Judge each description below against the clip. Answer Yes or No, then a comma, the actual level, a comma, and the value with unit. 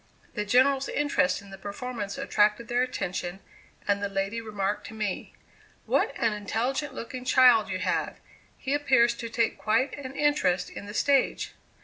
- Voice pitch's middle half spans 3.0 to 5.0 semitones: Yes, average, 4.3 semitones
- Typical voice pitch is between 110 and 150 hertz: No, high, 230 Hz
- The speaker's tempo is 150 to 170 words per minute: Yes, average, 160 wpm